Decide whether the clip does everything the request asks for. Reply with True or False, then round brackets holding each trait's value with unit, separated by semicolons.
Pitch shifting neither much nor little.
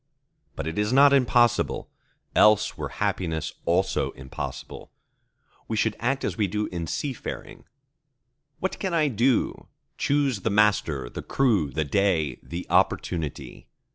False (7.2 semitones)